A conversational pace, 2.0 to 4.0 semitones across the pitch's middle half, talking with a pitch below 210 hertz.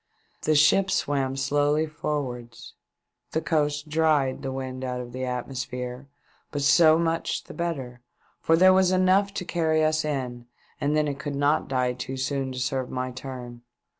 Yes: average, 165 wpm; average, 3.4 semitones; medium, 140 Hz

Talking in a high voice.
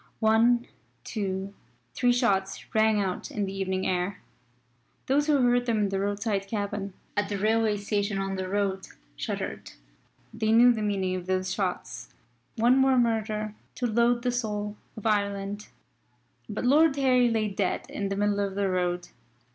Yes: high, 205 Hz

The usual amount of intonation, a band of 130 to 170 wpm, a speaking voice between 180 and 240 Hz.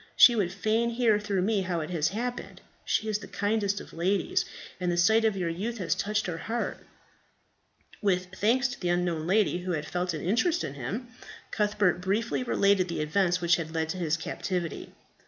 No: average, 3.8 semitones; average, 195 wpm; high, 190 Hz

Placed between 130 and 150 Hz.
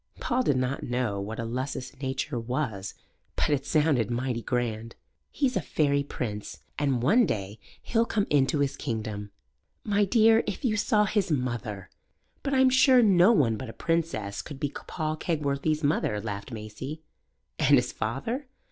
Yes: medium, 140 Hz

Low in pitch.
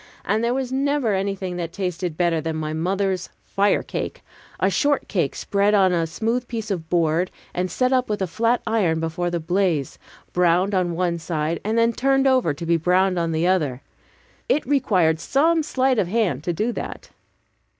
No: medium, 185 Hz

